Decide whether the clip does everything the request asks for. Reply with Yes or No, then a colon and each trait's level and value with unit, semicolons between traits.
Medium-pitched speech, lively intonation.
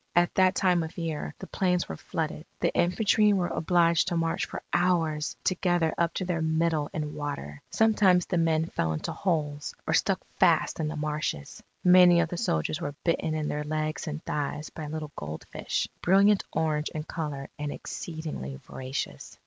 No: medium, 160 Hz; average, 2.8 semitones